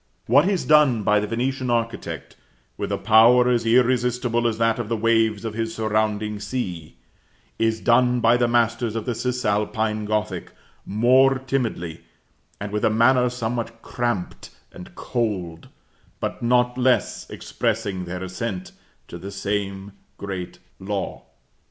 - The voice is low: Yes, low, 115 Hz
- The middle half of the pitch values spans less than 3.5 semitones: Yes, average, 2.9 semitones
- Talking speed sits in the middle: Yes, average, 145 wpm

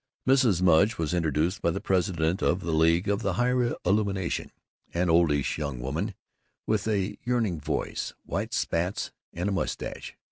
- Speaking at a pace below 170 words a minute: Yes, average, 155 wpm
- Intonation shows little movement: No, average, 3.7 semitones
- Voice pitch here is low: Yes, very low, 90 Hz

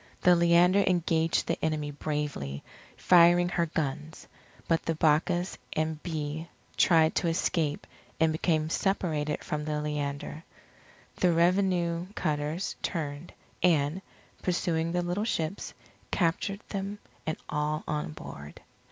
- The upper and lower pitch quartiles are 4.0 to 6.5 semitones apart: No, average, 2.7 semitones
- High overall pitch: No, medium, 160 Hz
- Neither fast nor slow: No, slow, 120 wpm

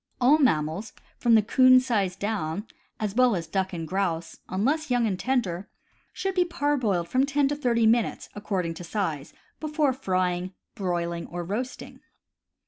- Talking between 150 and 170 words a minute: Yes, average, 155 wpm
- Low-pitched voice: No, high, 210 Hz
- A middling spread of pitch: No, wide, 6.3 semitones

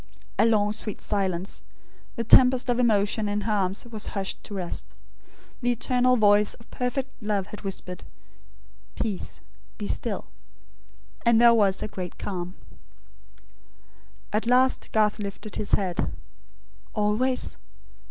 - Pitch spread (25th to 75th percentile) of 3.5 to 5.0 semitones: No, average, 2.9 semitones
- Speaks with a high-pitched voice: Yes, high, 210 Hz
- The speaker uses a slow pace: Yes, slow, 130 wpm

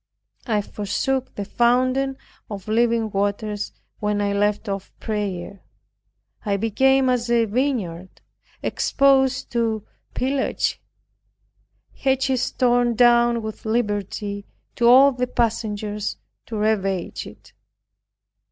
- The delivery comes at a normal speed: No, slow, 105 wpm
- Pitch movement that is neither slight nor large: Yes, average, 3.4 semitones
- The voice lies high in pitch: Yes, high, 225 Hz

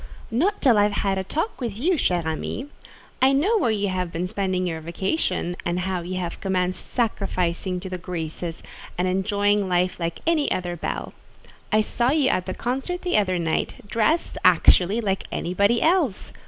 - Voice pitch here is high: Yes, high, 195 Hz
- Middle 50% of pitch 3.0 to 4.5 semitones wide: No, average, 5.0 semitones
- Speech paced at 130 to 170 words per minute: No, average, 180 wpm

